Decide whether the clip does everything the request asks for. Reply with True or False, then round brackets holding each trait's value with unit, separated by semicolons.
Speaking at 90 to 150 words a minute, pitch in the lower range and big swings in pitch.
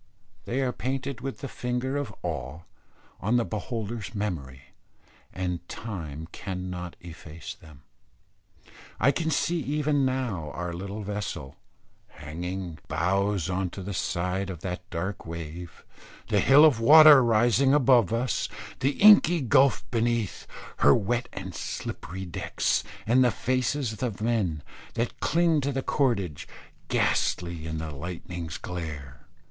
True (135 wpm; 100 Hz; 6.8 semitones)